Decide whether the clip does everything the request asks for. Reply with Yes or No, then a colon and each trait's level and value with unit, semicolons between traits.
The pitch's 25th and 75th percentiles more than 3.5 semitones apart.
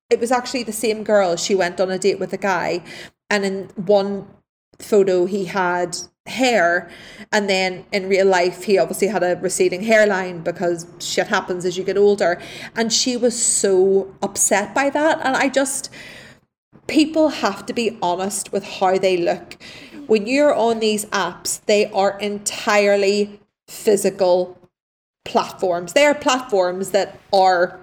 No: average, 2.9 semitones